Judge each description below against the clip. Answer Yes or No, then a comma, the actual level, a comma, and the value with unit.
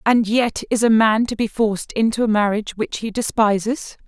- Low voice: No, high, 220 Hz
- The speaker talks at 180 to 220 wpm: Yes, fast, 205 wpm